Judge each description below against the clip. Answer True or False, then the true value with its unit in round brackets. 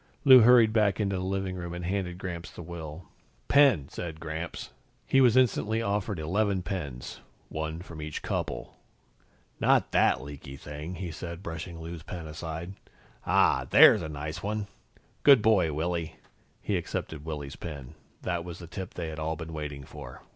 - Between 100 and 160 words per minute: False (170 wpm)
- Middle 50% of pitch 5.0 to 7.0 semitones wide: False (3.8 semitones)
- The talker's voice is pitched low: True (85 Hz)